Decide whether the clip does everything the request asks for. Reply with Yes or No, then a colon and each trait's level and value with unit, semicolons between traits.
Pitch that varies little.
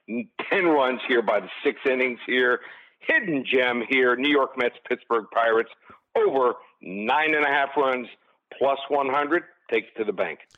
No: average, 3.0 semitones